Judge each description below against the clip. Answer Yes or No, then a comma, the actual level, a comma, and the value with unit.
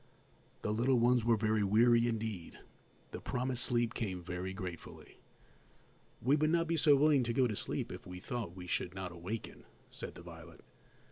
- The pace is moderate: Yes, average, 180 wpm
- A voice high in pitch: No, low, 110 Hz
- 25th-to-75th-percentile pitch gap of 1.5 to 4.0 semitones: No, average, 5.2 semitones